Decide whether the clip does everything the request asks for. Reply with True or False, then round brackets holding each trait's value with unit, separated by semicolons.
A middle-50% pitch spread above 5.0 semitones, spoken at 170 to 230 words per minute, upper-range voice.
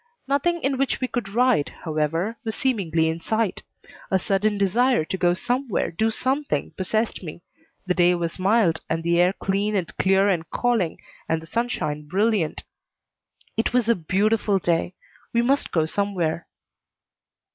False (5.4 semitones; 155 wpm; 195 Hz)